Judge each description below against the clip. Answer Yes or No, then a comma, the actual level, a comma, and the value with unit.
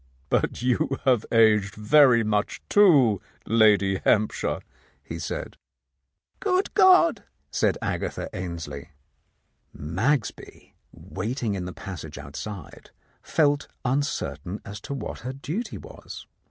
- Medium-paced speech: No, slow, 120 wpm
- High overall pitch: No, low, 110 Hz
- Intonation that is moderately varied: No, wide, 6.2 semitones